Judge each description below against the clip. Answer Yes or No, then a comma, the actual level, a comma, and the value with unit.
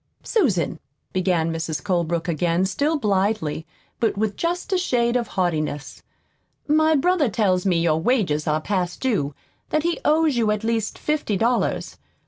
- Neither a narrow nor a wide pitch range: No, wide, 7.4 semitones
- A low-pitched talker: No, high, 205 Hz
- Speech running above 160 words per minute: No, average, 150 wpm